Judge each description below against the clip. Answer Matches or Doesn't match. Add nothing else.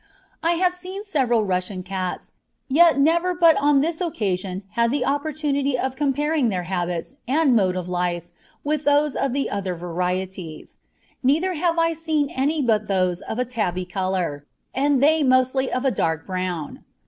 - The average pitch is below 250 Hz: Doesn't match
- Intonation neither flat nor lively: Doesn't match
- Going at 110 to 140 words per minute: Doesn't match